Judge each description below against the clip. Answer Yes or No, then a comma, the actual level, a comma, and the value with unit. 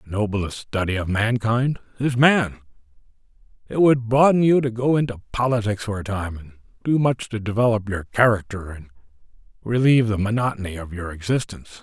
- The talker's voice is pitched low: Yes, low, 110 Hz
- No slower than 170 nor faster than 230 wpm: No, average, 160 wpm